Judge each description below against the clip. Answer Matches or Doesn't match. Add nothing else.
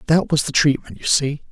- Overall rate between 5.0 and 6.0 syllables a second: Matches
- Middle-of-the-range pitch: Matches